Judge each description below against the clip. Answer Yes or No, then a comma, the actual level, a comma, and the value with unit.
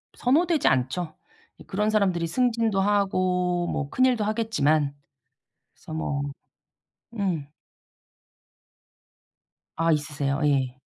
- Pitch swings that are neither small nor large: No, wide, 6.5 semitones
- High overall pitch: No, medium, 180 Hz